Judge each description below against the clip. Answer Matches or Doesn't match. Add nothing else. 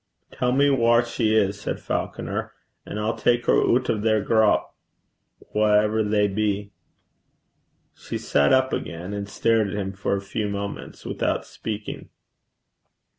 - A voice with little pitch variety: Matches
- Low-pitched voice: Matches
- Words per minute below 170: Matches